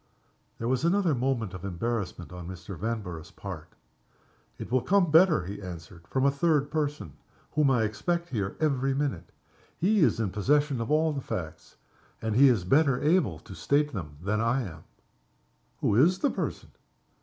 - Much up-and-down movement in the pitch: Yes, wide, 7.6 semitones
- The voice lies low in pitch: Yes, low, 125 Hz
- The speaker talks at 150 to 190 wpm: Yes, average, 170 wpm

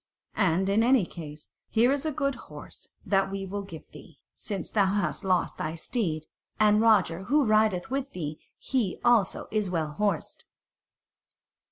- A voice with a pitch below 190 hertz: No, high, 200 Hz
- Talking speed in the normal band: Yes, average, 160 wpm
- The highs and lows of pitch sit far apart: No, average, 4.2 semitones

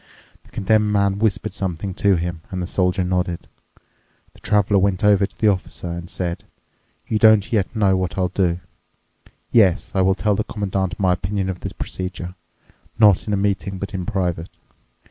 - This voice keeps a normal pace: Yes, average, 175 wpm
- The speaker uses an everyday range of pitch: No, narrow, 2.0 semitones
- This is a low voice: Yes, very low, 95 Hz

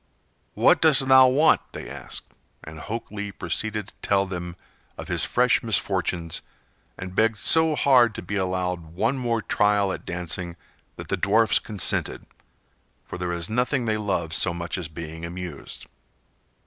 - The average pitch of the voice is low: Yes, low, 100 Hz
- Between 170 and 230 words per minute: No, average, 160 wpm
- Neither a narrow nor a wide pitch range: Yes, average, 4.6 semitones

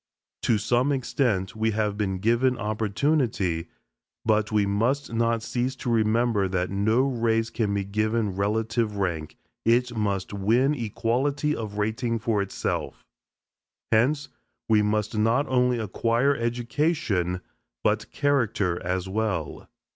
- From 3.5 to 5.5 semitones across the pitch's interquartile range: No, average, 3.0 semitones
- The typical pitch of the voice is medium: No, low, 110 Hz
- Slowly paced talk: Yes, slow, 125 wpm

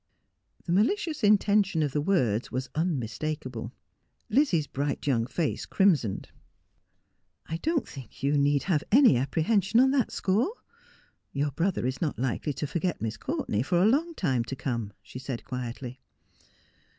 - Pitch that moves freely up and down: Yes, wide, 7.4 semitones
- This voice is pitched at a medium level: Yes, medium, 150 Hz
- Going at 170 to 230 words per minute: No, average, 150 wpm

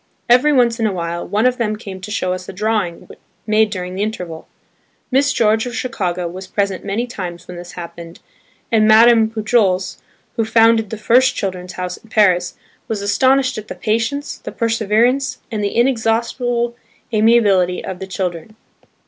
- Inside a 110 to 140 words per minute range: No, average, 170 wpm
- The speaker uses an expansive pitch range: No, average, 3.9 semitones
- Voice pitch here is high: Yes, high, 215 Hz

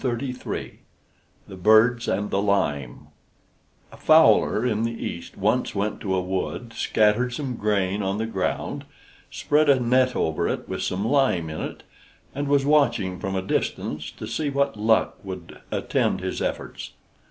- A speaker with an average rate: Yes, average, 155 wpm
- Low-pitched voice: Yes, low, 110 Hz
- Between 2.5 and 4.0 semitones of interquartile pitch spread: No, average, 4.8 semitones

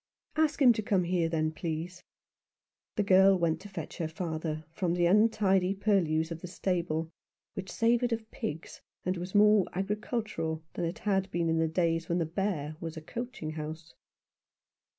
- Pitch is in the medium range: Yes, medium, 180 Hz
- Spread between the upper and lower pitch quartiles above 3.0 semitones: Yes, average, 3.7 semitones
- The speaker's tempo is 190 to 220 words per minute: No, average, 170 wpm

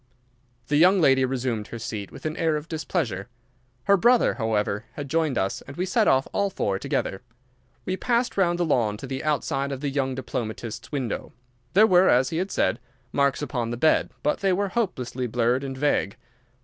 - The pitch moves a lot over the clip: Yes, wide, 6.3 semitones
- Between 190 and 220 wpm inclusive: Yes, average, 195 wpm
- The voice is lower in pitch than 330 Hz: Yes, medium, 140 Hz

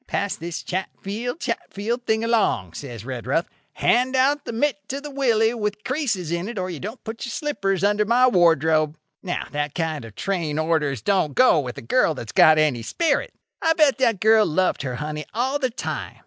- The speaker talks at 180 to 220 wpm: Yes, average, 190 wpm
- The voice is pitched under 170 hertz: No, high, 195 Hz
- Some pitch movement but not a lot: No, wide, 7.6 semitones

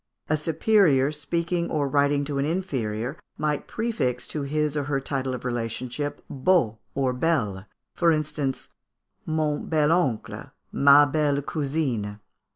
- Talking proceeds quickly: No, slow, 135 wpm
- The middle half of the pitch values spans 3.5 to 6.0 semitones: No, average, 3.0 semitones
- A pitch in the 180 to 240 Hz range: No, medium, 145 Hz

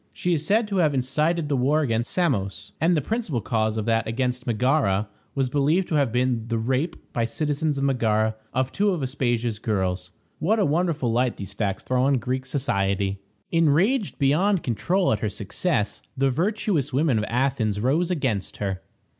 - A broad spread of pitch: Yes, wide, 5.8 semitones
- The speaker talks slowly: No, average, 180 wpm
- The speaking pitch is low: Yes, low, 130 Hz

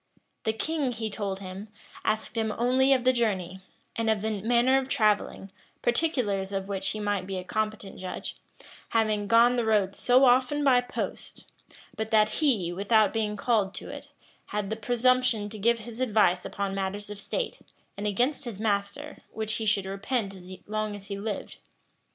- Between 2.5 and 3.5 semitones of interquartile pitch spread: Yes, average, 3.2 semitones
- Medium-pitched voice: No, high, 215 Hz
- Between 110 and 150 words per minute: No, average, 180 wpm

